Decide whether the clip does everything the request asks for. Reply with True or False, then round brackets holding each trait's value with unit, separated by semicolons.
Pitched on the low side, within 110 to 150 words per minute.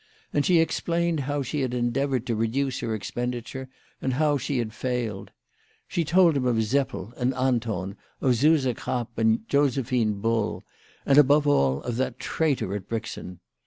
False (125 Hz; 170 wpm)